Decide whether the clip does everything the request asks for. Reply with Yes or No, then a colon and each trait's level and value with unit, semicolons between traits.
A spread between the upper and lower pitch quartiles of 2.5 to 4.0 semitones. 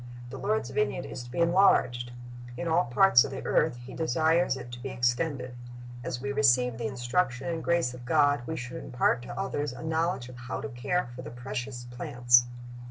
No: average, 4.8 semitones